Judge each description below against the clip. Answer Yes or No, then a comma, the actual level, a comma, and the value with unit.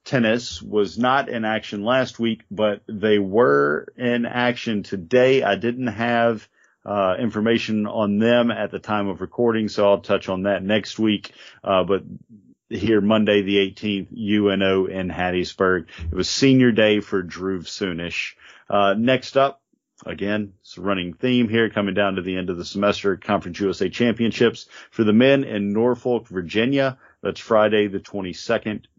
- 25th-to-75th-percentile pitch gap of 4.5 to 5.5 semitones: No, average, 3.0 semitones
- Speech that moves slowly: No, average, 160 wpm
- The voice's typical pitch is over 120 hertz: No, low, 105 Hz